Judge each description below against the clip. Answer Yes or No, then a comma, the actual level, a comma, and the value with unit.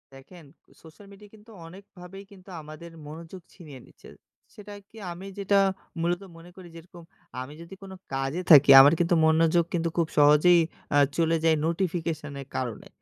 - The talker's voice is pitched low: No, medium, 170 Hz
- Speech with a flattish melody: No, average, 3.2 semitones